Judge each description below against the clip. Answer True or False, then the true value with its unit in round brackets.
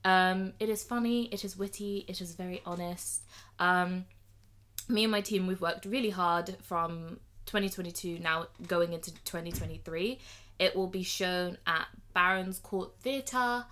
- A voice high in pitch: False (180 Hz)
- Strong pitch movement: False (2.9 semitones)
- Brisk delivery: False (150 wpm)